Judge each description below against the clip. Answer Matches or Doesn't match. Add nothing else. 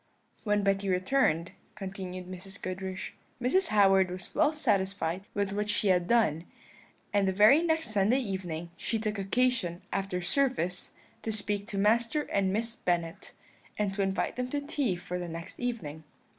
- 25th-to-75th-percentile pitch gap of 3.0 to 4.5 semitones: Matches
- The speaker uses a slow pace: Doesn't match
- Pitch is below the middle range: Doesn't match